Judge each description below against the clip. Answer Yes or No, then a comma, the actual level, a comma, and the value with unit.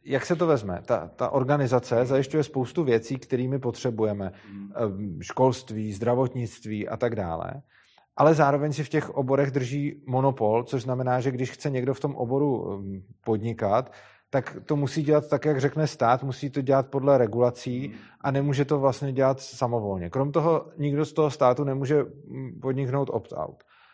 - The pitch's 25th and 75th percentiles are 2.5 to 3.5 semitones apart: Yes, average, 2.9 semitones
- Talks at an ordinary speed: Yes, average, 160 wpm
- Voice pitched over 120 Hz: Yes, low, 135 Hz